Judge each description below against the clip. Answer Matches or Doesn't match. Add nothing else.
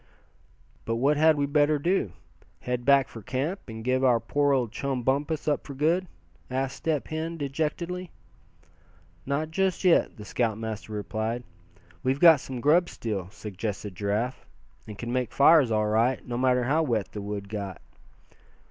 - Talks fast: Doesn't match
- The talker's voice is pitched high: Doesn't match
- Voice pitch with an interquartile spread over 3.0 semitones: Matches